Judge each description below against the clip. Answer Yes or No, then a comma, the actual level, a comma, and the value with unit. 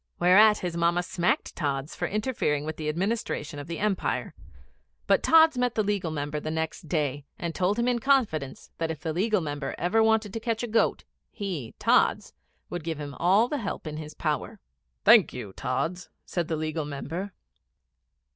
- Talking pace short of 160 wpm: No, average, 185 wpm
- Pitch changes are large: Yes, wide, 5.7 semitones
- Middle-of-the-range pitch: Yes, medium, 175 Hz